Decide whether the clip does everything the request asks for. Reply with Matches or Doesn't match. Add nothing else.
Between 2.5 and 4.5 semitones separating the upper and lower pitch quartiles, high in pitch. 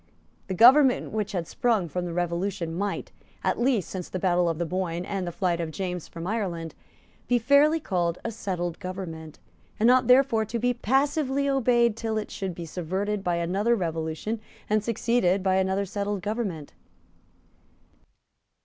Doesn't match